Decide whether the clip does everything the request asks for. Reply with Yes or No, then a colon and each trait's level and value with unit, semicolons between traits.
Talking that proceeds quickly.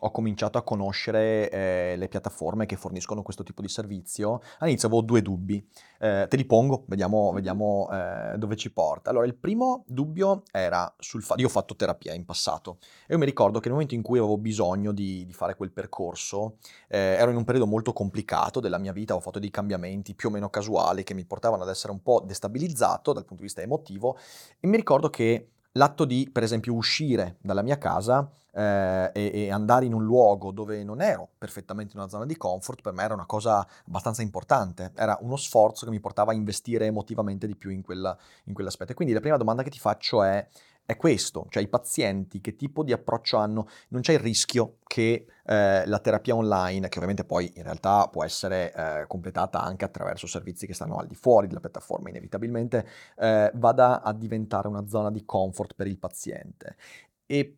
Yes: fast, 205 wpm